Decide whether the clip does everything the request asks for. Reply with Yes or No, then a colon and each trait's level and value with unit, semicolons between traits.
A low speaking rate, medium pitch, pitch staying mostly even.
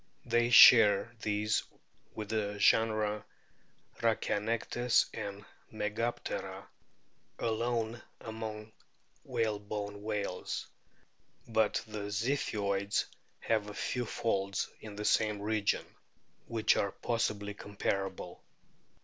No: slow, 90 wpm; low, 105 Hz; narrow, 1.7 semitones